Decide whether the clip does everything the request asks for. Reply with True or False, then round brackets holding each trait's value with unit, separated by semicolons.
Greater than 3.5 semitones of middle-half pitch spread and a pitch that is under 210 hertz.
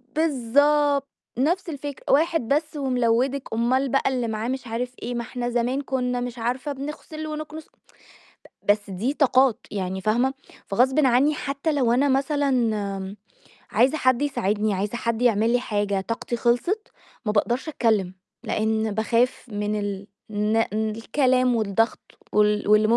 False (4.1 semitones; 245 Hz)